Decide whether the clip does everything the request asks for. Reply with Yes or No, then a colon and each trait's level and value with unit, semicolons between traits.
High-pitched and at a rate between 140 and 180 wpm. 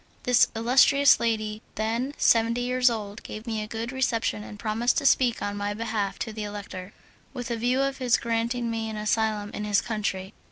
No: high, 225 Hz; average, 195 wpm